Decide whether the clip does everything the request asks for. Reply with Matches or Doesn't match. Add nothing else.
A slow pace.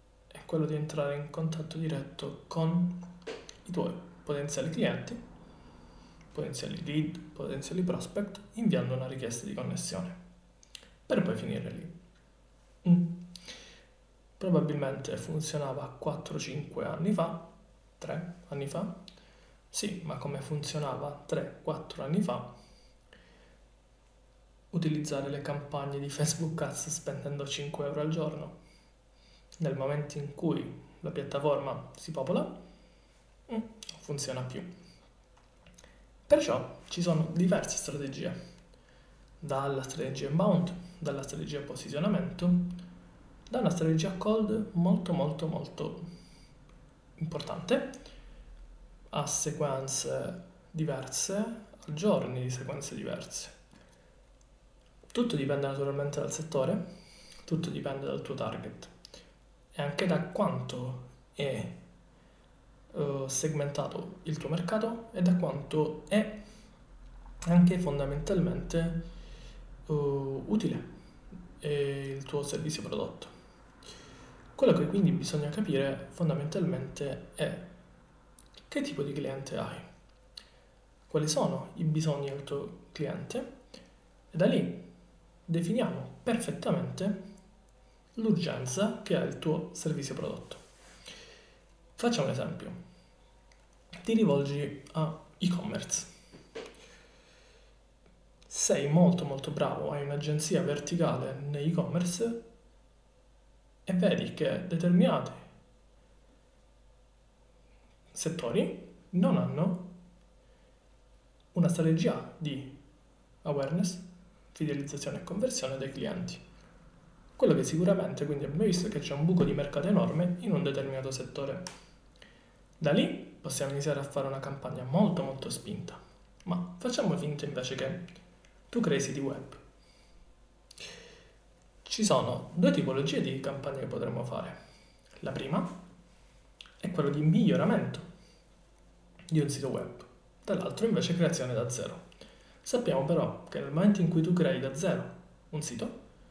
Matches